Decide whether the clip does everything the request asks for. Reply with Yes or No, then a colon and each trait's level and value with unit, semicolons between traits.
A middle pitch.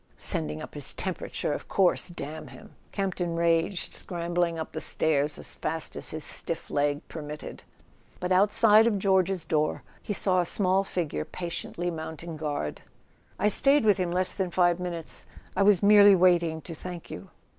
Yes: medium, 175 Hz